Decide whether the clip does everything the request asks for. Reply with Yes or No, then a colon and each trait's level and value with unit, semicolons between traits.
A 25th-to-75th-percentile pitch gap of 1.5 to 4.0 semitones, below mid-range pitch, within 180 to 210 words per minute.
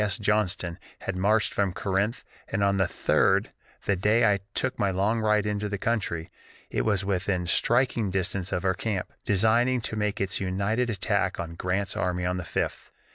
Yes: narrow, 2.6 semitones; low, 100 Hz; average, 185 wpm